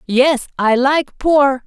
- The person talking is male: No, female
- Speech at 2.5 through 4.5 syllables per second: Yes, 2.9 syllables/s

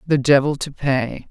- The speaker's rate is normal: Yes, average, 185 wpm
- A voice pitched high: No, medium, 140 Hz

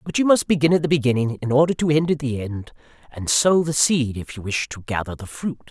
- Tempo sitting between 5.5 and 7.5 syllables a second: Yes, 5.9 syllables/s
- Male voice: Yes, male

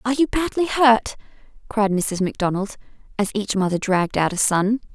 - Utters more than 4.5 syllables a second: Yes, 5.5 syllables/s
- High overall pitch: Yes, high, 215 Hz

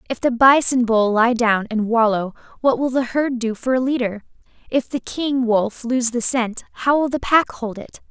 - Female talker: Yes, female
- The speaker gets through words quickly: Yes, fast, 215 wpm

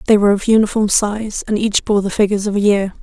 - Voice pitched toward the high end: Yes, high, 205 Hz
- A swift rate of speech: Yes, fast, 260 wpm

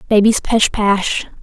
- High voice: Yes, high, 210 Hz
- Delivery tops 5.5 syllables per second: No, 3.6 syllables/s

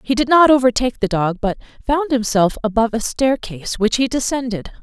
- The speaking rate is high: No, average, 185 wpm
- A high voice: Yes, high, 240 Hz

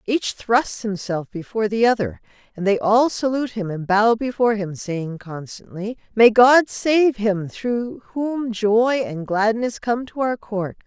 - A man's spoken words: No, female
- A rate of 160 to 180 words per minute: Yes, average, 165 wpm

